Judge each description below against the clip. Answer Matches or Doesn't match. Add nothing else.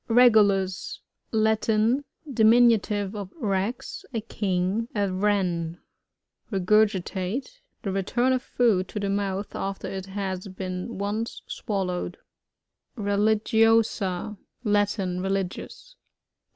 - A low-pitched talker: Doesn't match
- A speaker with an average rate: Doesn't match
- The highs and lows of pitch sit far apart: Doesn't match